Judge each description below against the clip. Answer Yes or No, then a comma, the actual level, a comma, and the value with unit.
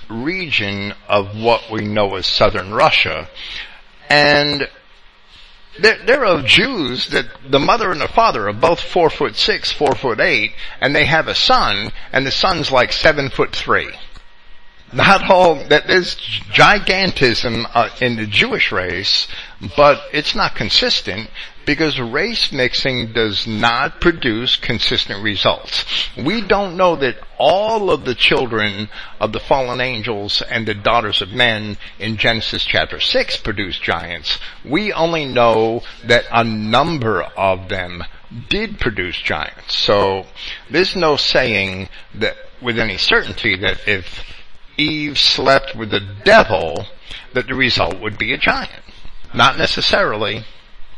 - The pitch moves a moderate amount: No, wide, 5.8 semitones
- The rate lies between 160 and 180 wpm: No, average, 140 wpm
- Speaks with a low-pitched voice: Yes, low, 115 Hz